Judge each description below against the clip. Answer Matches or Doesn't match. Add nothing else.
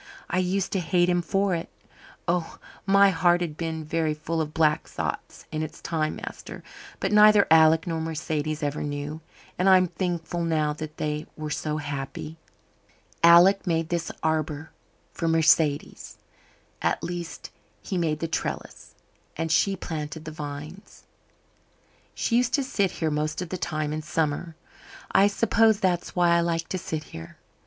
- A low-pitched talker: Doesn't match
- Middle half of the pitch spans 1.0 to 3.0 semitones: Matches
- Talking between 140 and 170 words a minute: Matches